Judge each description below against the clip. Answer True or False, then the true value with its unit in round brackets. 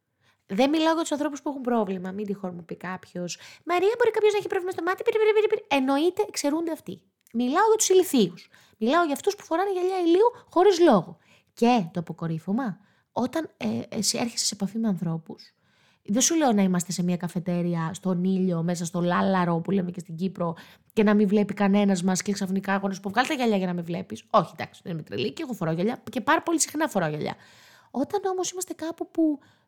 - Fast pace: True (210 wpm)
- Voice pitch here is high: True (220 Hz)